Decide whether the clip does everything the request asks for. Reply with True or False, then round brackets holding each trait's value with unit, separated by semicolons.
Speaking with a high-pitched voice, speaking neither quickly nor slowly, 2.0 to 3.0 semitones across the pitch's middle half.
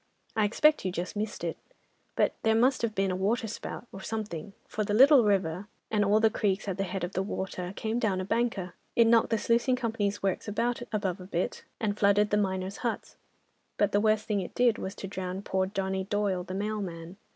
False (205 Hz; 210 wpm; 2.7 semitones)